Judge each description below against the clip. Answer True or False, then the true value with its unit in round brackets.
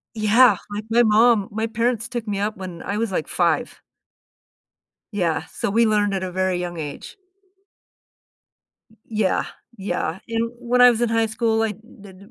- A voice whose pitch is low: False (215 Hz)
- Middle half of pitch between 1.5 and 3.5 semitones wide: True (3.2 semitones)